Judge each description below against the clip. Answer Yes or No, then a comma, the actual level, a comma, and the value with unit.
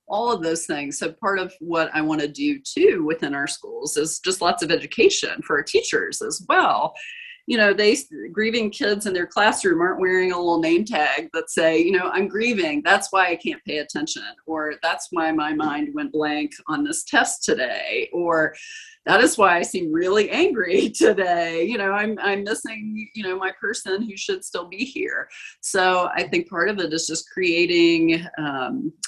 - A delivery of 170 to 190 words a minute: No, average, 200 wpm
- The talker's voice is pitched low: No, high, 210 Hz